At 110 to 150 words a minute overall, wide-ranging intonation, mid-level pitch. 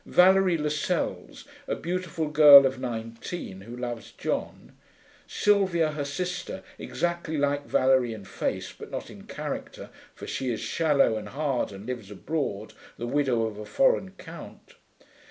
Yes: average, 145 wpm; wide, 5.9 semitones; medium, 145 Hz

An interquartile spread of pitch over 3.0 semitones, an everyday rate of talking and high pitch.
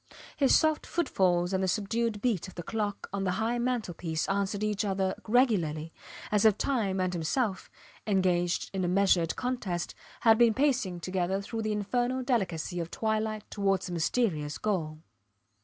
Yes: average, 3.9 semitones; average, 165 wpm; high, 200 Hz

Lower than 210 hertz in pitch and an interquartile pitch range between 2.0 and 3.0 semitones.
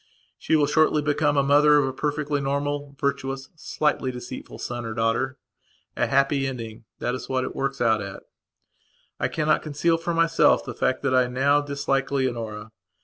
Yes: low, 135 Hz; narrow, 2.6 semitones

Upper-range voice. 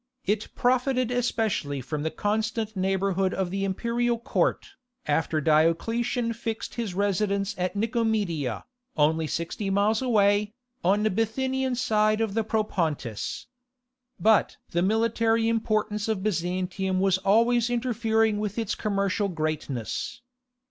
Yes: high, 210 Hz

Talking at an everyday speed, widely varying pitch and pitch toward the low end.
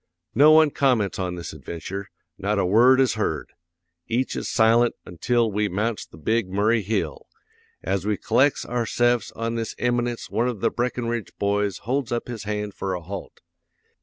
No: average, 170 wpm; average, 3.5 semitones; low, 110 Hz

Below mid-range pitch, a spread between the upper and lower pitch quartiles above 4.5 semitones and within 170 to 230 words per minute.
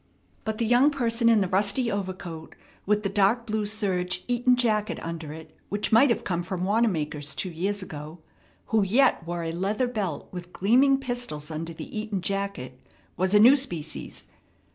No: high, 200 Hz; average, 4.9 semitones; average, 175 wpm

